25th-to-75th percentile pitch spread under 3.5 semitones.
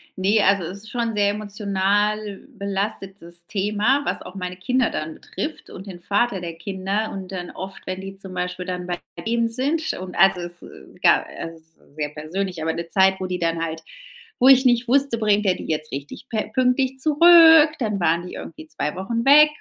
No: average, 4.4 semitones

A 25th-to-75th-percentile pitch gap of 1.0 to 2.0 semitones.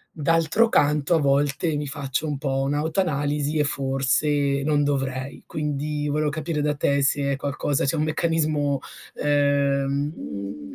Yes: narrow, 1.5 semitones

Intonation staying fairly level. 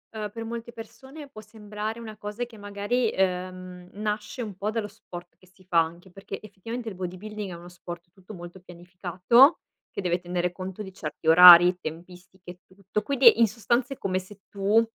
No: average, 3.4 semitones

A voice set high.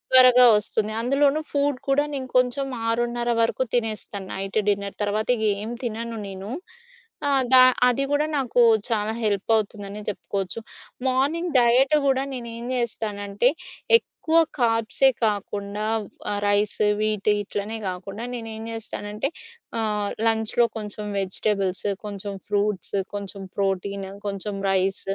Yes: high, 215 Hz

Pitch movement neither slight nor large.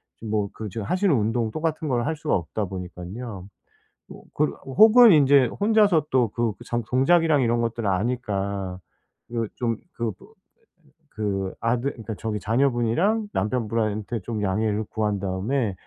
Yes: average, 4.7 semitones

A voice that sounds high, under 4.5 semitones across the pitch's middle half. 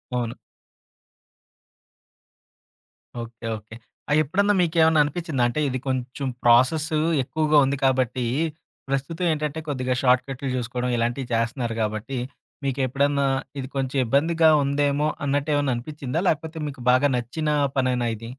No: low, 135 Hz; average, 3.2 semitones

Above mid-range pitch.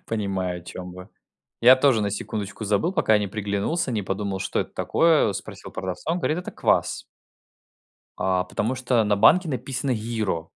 No: low, 105 Hz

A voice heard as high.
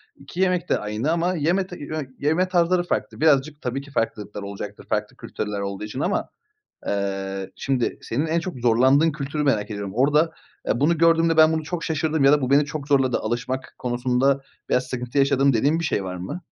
No: medium, 140 Hz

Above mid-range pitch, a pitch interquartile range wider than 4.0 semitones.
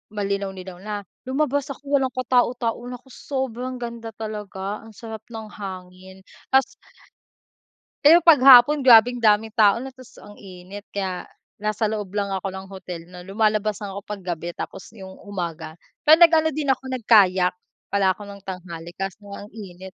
Yes: high, 210 Hz; average, 4.4 semitones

